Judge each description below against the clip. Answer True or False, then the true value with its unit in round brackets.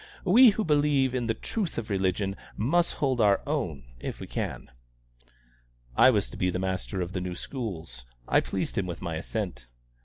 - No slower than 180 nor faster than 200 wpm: True (185 wpm)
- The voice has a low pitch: True (105 Hz)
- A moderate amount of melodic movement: False (6.9 semitones)